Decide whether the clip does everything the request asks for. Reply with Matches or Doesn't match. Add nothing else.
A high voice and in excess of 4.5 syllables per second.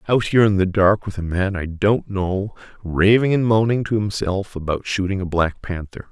Doesn't match